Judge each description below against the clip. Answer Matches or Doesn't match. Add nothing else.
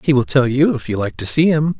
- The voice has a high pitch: Doesn't match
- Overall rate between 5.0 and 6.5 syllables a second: Matches